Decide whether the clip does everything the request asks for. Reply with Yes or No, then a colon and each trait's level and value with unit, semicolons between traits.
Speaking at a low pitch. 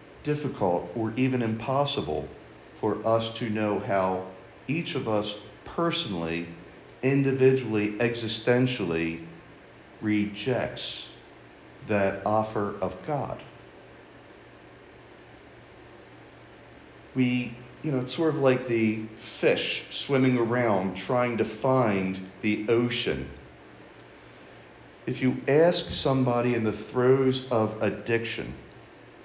Yes: low, 115 Hz